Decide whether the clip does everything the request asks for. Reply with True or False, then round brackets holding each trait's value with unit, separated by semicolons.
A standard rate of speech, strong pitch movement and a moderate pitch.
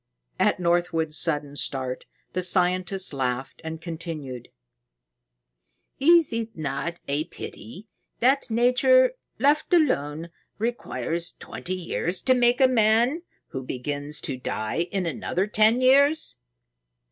False (115 wpm; 8.5 semitones; 180 Hz)